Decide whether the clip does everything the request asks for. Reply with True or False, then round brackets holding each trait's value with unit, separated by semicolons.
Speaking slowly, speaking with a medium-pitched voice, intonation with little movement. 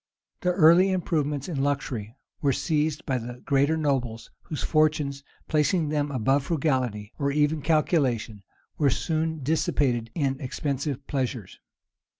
False (130 wpm; 145 Hz; 3.0 semitones)